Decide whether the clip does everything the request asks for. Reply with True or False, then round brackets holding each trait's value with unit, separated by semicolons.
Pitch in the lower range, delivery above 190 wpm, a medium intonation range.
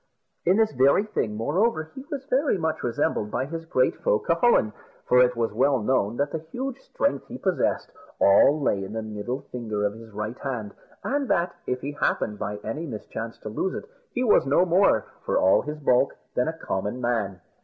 False (130 Hz; 200 wpm; 7.6 semitones)